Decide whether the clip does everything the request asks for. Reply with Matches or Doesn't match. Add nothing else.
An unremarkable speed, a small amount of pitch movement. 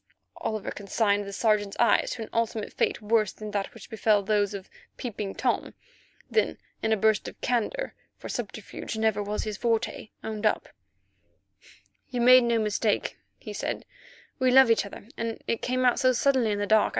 Matches